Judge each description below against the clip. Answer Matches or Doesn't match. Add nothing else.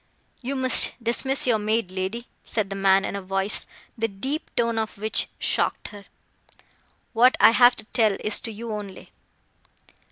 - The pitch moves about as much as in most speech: Matches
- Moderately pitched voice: Doesn't match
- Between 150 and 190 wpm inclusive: Matches